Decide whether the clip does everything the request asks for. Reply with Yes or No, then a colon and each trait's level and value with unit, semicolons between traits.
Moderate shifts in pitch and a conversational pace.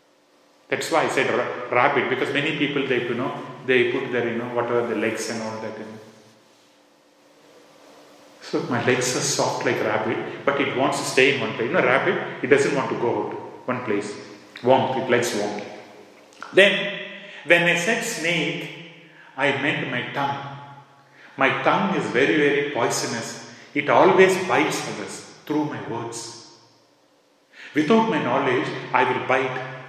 Yes: average, 5.0 semitones; average, 165 wpm